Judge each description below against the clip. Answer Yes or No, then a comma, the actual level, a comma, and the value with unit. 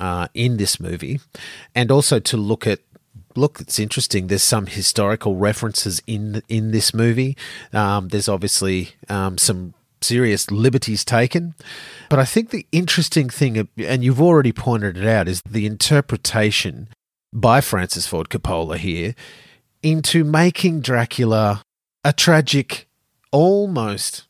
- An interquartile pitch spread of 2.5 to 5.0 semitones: No, wide, 5.5 semitones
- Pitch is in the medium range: No, low, 115 Hz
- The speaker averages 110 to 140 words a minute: Yes, slow, 135 wpm